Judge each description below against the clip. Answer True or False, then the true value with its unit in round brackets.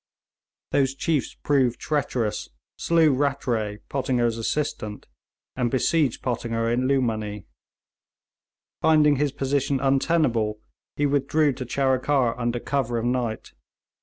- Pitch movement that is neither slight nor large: True (3.4 semitones)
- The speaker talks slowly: True (105 wpm)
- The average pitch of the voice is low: True (130 Hz)